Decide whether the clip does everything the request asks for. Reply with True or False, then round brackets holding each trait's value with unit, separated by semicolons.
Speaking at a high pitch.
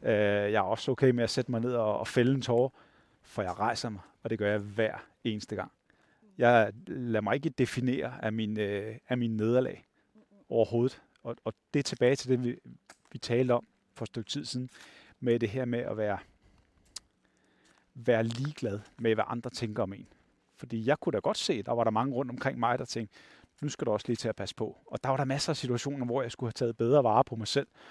False (120 Hz)